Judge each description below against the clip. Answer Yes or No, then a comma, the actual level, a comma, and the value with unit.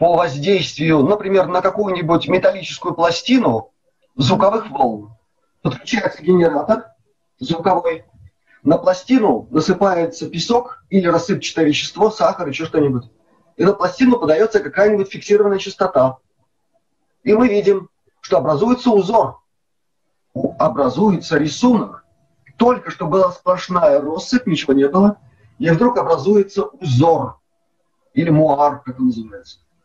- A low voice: No, medium, 180 Hz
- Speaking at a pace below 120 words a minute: Yes, slow, 110 wpm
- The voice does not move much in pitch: No, average, 5.1 semitones